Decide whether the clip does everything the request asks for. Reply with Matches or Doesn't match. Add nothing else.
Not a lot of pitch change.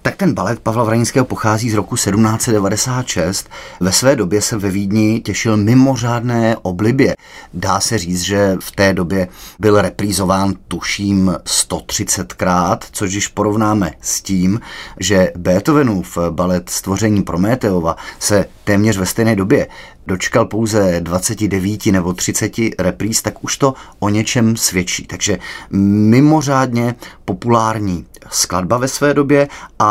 Doesn't match